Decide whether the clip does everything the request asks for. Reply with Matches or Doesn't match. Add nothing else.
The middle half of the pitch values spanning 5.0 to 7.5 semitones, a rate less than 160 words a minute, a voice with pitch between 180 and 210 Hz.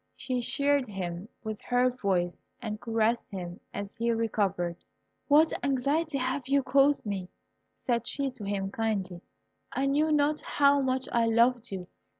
Doesn't match